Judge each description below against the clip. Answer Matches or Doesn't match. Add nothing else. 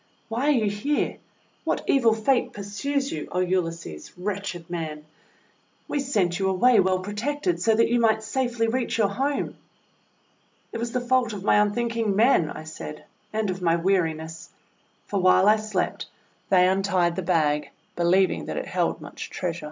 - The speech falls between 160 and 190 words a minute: Matches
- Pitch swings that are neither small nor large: Matches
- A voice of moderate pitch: Doesn't match